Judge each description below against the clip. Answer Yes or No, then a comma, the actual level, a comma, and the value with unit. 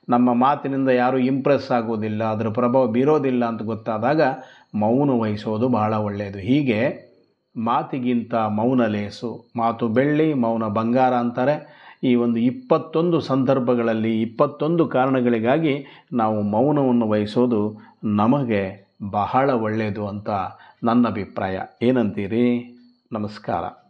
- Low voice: Yes, low, 120 Hz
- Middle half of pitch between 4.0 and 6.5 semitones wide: No, average, 3.0 semitones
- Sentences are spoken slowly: No, average, 100 wpm